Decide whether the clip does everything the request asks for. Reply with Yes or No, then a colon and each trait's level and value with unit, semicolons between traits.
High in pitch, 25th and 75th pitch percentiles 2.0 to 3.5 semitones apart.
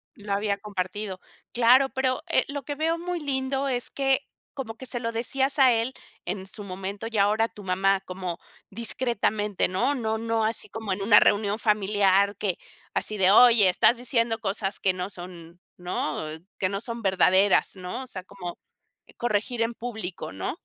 No: high, 210 Hz; average, 3.9 semitones